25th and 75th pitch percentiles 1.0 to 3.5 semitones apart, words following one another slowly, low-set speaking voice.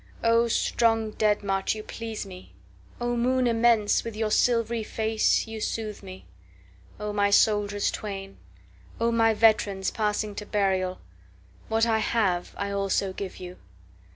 No: average, 2.8 semitones; slow, 130 wpm; high, 210 Hz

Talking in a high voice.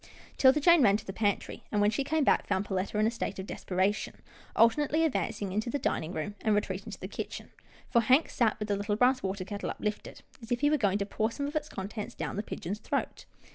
Yes: high, 215 Hz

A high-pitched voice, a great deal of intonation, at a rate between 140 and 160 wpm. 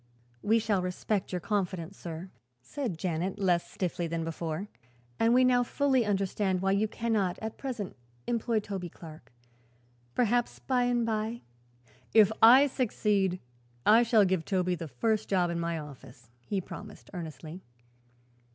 No: high, 195 Hz; average, 4.7 semitones; average, 150 wpm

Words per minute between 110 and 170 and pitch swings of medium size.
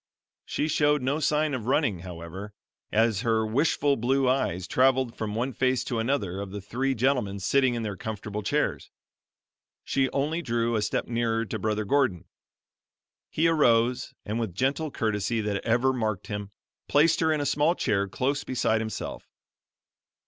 Yes: average, 165 wpm; average, 4.4 semitones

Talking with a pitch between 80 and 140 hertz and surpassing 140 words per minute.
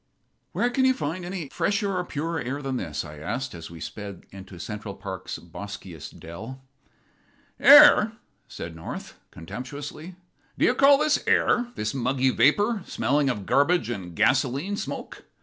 Yes: low, 135 Hz; average, 150 wpm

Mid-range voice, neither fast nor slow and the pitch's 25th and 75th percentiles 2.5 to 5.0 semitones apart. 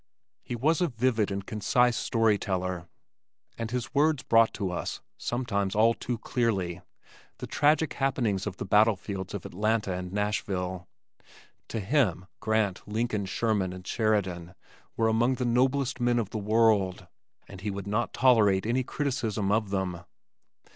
No: low, 110 Hz; average, 150 wpm; average, 3.8 semitones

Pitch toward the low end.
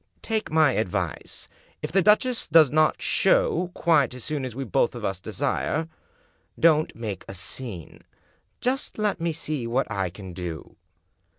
No: medium, 150 Hz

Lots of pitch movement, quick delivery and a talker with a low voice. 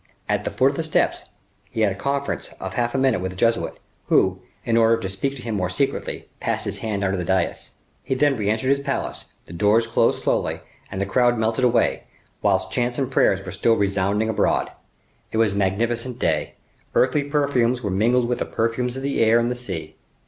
No: average, 4.2 semitones; fast, 215 wpm; low, 115 Hz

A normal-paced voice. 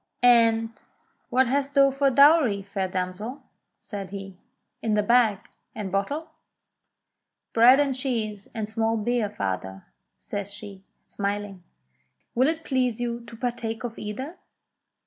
No: slow, 130 wpm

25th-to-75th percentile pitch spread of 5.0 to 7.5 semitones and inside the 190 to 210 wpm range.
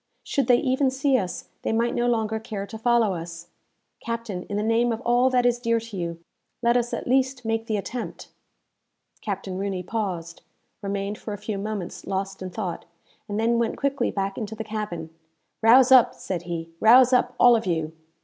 No: average, 3.6 semitones; average, 195 wpm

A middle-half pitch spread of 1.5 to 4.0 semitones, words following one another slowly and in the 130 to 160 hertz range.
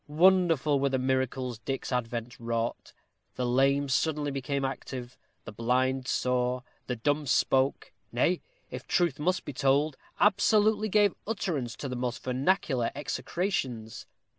Yes: average, 3.7 semitones; slow, 130 wpm; low, 135 Hz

